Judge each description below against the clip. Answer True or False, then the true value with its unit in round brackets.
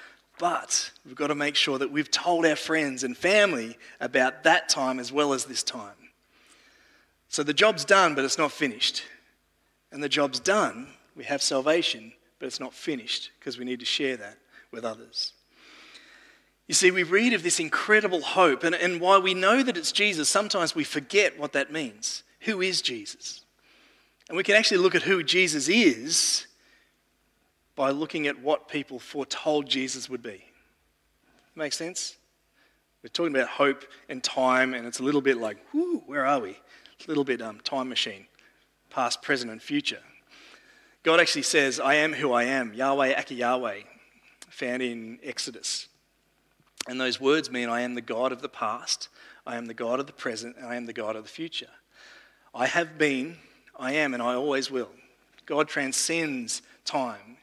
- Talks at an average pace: True (180 wpm)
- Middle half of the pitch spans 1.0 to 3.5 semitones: False (5.3 semitones)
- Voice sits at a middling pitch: True (145 Hz)